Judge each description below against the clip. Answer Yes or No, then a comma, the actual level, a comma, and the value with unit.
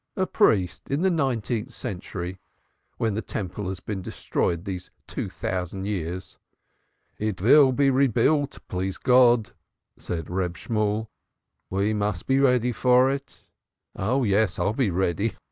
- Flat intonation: No, wide, 5.4 semitones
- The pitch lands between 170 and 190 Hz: No, low, 105 Hz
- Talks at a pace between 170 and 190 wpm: No, average, 145 wpm